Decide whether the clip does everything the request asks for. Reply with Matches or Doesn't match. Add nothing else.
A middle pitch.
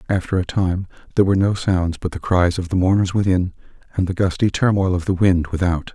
Doesn't match